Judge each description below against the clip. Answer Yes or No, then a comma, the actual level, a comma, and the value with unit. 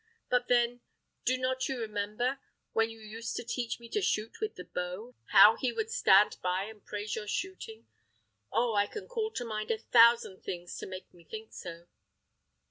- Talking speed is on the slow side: No, average, 190 wpm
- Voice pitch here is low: No, high, 225 Hz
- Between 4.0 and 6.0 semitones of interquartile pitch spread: No, average, 3.4 semitones